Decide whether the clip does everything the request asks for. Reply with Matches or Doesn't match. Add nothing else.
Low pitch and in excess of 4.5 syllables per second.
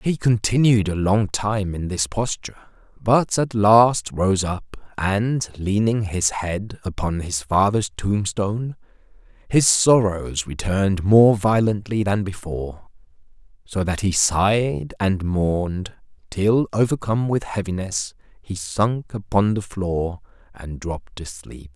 Doesn't match